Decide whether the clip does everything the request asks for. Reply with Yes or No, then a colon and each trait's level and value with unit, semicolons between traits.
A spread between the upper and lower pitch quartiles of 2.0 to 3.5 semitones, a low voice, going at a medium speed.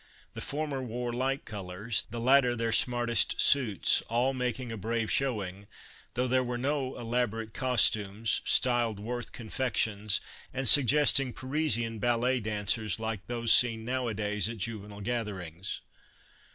No: average, 2.9 semitones; low, 115 Hz; slow, 130 wpm